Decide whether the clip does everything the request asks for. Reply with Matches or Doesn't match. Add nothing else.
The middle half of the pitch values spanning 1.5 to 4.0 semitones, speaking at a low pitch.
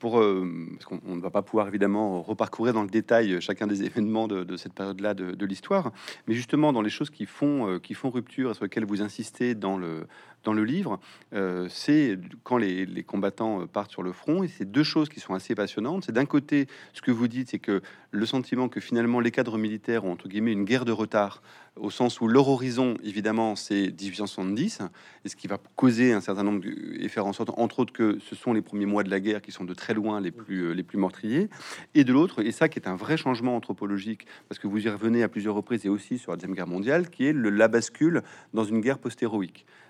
Matches